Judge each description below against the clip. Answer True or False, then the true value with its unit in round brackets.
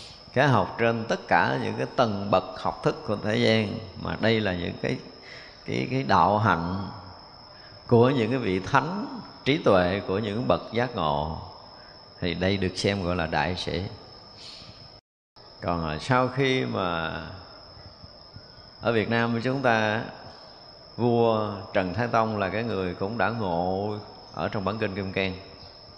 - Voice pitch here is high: False (100 Hz)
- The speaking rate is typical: False (155 wpm)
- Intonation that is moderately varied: True (3.9 semitones)